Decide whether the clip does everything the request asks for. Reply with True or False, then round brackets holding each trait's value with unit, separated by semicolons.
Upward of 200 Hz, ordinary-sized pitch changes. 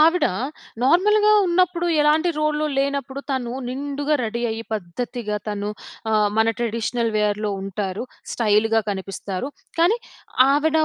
False (245 Hz; 6.3 semitones)